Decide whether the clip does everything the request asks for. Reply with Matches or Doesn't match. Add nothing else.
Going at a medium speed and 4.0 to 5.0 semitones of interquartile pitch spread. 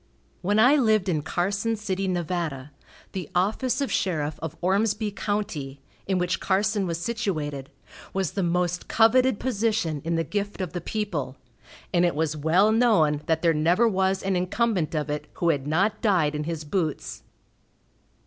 Matches